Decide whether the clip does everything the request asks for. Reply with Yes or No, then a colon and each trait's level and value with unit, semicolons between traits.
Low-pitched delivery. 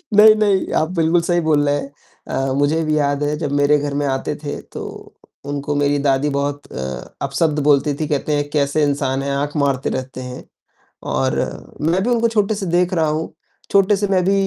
No: medium, 150 Hz